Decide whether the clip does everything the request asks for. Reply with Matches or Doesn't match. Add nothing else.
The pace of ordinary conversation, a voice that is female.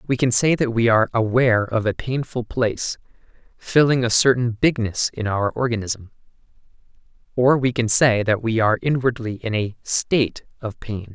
Doesn't match